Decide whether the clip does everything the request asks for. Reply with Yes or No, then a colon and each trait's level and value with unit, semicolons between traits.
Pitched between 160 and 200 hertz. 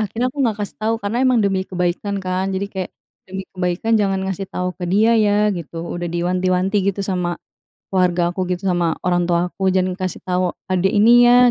Yes: medium, 185 Hz